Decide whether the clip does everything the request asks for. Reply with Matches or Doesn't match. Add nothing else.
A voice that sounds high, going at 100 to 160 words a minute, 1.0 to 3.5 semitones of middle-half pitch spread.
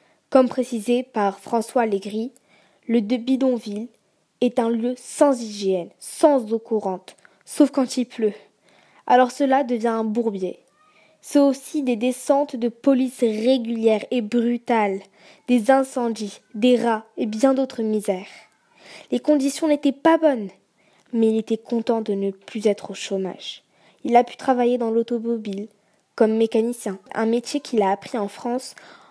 Matches